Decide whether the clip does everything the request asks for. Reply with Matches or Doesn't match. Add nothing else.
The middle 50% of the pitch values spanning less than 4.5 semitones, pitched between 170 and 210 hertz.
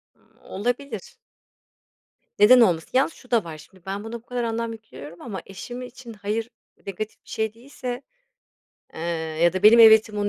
Doesn't match